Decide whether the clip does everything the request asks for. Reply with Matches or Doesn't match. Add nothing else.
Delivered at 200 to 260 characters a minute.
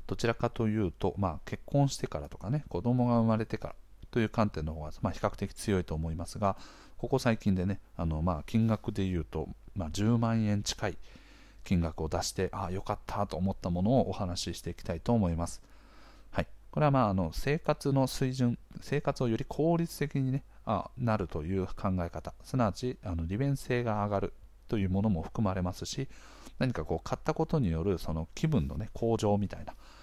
Doesn't match